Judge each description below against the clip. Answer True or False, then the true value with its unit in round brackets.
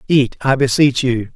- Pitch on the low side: True (130 Hz)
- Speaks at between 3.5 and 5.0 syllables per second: True (4.5 syllables/s)